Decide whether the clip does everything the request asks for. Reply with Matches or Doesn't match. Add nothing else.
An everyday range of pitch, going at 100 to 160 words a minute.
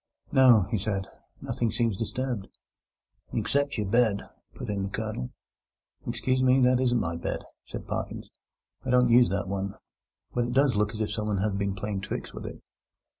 Doesn't match